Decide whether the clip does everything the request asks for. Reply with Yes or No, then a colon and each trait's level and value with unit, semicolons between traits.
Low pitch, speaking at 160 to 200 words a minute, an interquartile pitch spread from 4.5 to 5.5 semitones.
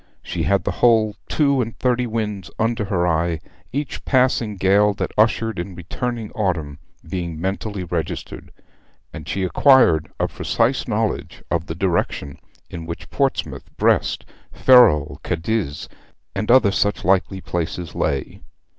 No: low, 100 Hz; slow, 135 wpm; average, 5.0 semitones